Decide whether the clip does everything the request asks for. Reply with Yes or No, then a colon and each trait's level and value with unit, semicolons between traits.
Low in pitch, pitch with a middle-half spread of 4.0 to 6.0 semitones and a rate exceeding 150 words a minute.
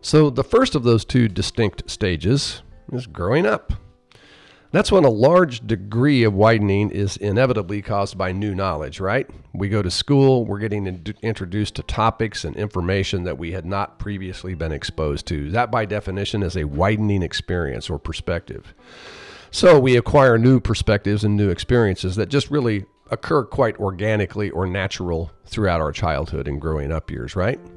No: low, 100 Hz; average, 3.5 semitones; average, 170 wpm